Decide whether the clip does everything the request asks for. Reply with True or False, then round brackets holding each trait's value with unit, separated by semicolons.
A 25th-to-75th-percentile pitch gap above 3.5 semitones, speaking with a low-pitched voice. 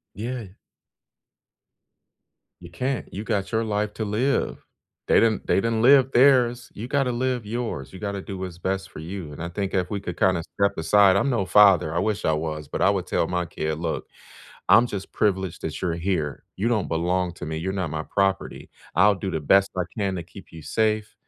True (4.0 semitones; 95 Hz)